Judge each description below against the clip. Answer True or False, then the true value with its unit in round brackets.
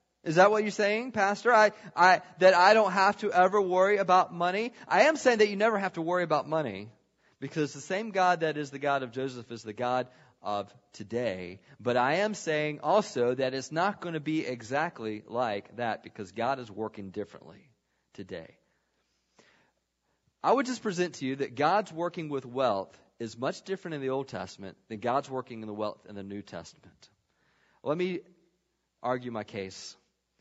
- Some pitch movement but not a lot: False (7.9 semitones)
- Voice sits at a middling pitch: True (145 Hz)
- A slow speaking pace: False (190 wpm)